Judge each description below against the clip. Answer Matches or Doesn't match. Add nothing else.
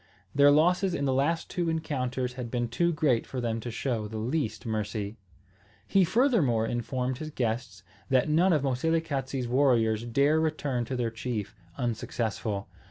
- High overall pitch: Doesn't match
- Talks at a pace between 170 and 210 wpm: Doesn't match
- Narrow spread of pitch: Doesn't match